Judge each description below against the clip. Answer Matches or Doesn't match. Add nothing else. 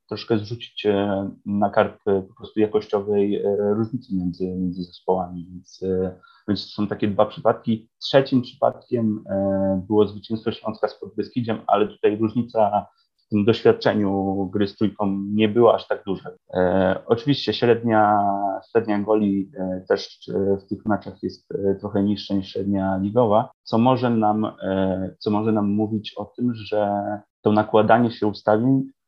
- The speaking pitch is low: Matches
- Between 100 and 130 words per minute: Doesn't match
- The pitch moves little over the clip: Matches